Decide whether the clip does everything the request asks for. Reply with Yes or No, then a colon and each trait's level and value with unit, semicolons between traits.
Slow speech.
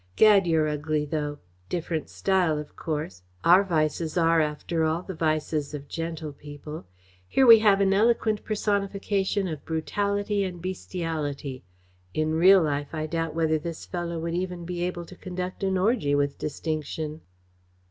No: average, 155 wpm